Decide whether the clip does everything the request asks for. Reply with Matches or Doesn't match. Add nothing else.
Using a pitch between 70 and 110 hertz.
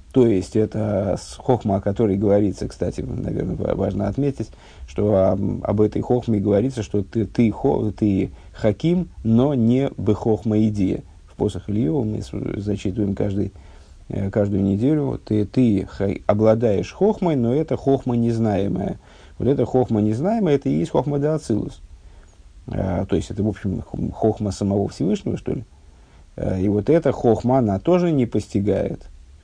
Matches